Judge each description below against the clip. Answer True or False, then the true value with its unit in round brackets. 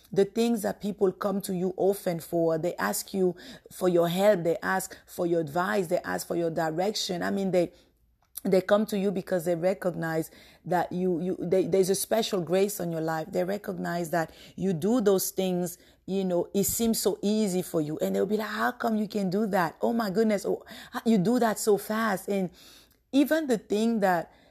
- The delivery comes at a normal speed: False (210 wpm)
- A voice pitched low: False (190 Hz)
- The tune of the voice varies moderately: True (3.0 semitones)